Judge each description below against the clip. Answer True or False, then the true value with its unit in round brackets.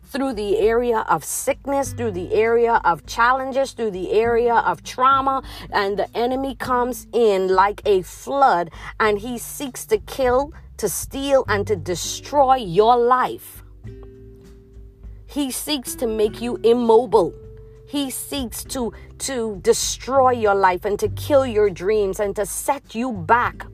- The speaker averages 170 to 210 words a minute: False (145 wpm)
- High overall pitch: True (240 Hz)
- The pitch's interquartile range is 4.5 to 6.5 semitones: True (5.0 semitones)